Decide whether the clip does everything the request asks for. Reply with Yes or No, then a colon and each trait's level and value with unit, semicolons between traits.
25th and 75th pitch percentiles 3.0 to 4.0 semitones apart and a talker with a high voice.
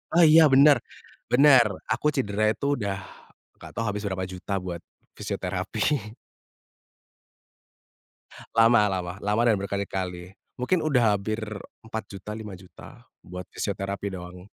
No: average, 3.6 semitones; low, 105 Hz